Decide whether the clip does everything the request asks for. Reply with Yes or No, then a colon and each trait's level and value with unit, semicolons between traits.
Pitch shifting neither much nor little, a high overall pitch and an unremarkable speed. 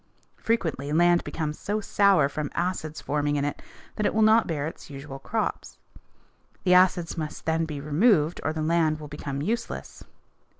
No: average, 3.8 semitones; medium, 160 Hz; average, 170 wpm